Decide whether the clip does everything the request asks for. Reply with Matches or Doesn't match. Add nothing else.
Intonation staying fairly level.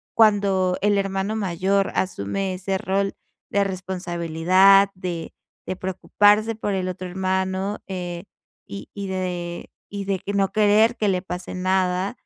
Matches